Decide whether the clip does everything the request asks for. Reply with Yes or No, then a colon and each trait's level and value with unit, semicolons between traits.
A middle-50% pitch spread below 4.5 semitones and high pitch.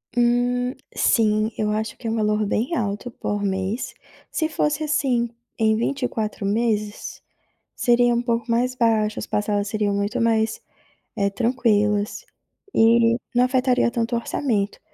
Yes: narrow, 2.5 semitones; high, 230 Hz